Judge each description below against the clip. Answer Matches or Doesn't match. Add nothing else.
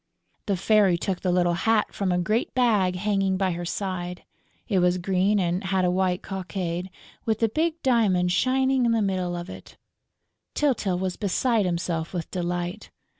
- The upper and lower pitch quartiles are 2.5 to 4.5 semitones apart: Matches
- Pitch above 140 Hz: Matches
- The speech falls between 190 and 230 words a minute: Doesn't match